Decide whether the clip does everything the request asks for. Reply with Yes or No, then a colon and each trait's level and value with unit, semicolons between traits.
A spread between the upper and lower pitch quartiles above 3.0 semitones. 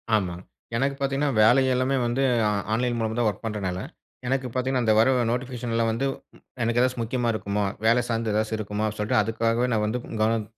No: average, 2.7 semitones